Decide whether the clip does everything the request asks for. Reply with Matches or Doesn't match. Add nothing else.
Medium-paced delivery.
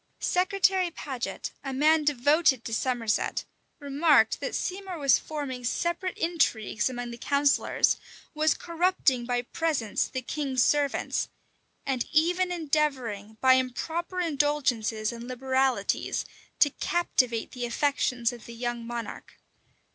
Doesn't match